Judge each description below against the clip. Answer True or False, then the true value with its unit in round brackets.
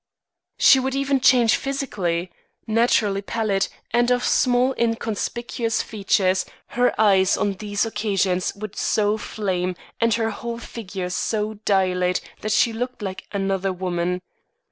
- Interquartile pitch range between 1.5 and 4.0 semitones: True (3.7 semitones)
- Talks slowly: True (130 wpm)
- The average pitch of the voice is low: False (210 Hz)